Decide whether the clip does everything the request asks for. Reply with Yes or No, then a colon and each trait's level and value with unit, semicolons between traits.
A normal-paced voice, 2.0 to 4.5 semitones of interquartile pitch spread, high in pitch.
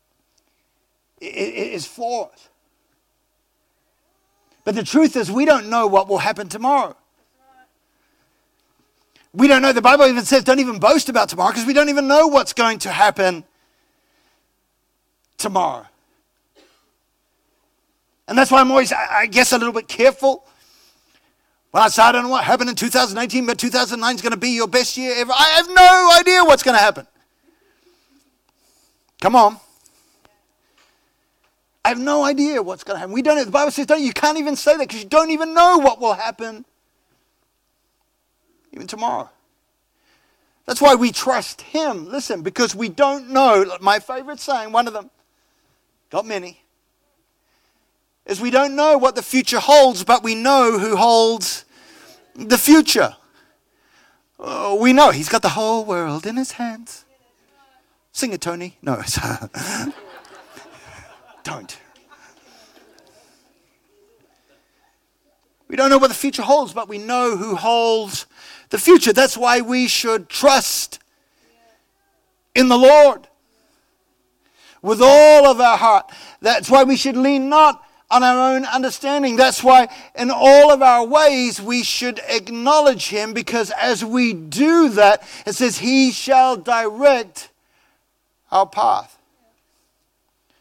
Yes: average, 145 wpm; average, 4.2 semitones; very high, 260 Hz